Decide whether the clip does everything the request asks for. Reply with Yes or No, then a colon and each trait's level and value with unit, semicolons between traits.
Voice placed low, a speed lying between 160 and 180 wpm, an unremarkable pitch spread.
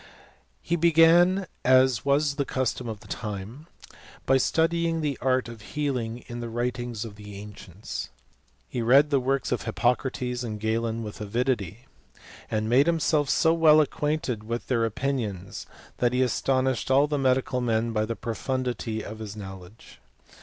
Yes: low, 125 Hz; average, 165 wpm; average, 4.0 semitones